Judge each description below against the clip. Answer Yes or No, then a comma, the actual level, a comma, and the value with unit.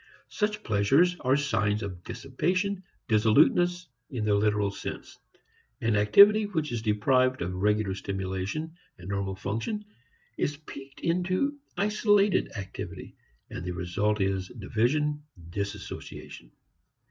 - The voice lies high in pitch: No, low, 110 Hz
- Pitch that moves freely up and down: Yes, wide, 9.0 semitones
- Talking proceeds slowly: Yes, slow, 115 wpm